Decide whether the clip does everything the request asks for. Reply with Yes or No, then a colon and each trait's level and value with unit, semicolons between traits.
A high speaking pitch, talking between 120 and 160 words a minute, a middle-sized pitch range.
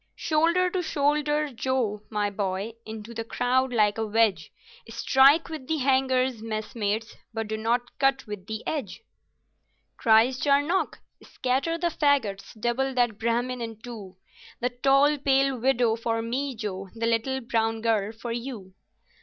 Yes: high, 240 Hz; average, 145 wpm; average, 3.5 semitones